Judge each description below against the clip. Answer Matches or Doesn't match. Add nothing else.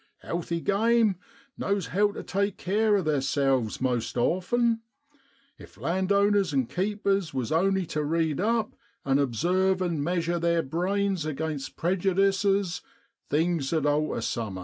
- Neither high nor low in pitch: Matches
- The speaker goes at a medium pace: Doesn't match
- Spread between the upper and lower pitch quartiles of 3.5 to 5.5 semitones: Matches